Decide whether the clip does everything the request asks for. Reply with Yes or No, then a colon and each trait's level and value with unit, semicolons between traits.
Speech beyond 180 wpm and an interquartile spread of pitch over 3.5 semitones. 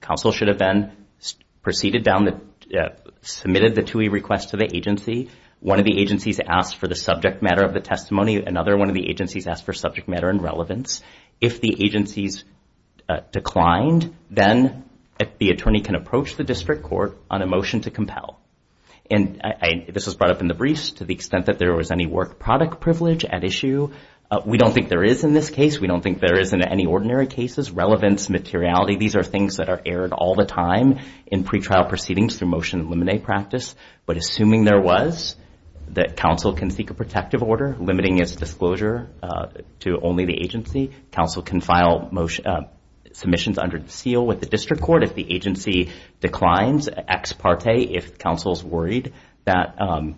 Yes: average, 190 wpm; average, 3.9 semitones